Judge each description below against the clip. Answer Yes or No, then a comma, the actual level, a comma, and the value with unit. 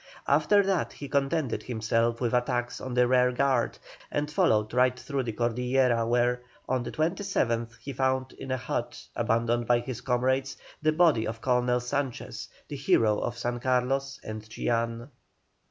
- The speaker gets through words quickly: No, average, 160 wpm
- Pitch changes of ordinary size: No, narrow, 2.3 semitones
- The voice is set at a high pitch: No, low, 125 Hz